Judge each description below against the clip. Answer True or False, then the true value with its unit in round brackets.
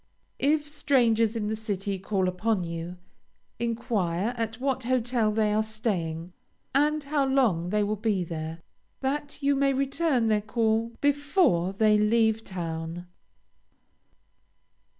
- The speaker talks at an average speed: False (130 wpm)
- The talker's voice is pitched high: True (220 Hz)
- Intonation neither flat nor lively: False (5.7 semitones)